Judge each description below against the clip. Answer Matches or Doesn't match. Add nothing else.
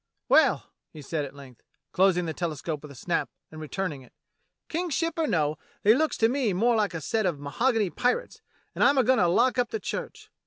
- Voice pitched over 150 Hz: Matches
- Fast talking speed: Matches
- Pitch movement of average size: Doesn't match